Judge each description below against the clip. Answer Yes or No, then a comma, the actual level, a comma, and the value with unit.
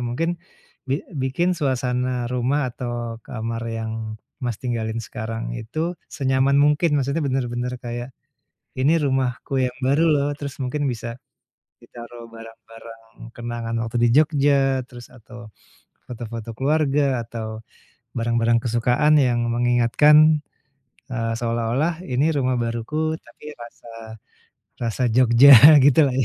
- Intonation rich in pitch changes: No, average, 3.1 semitones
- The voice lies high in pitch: No, low, 125 Hz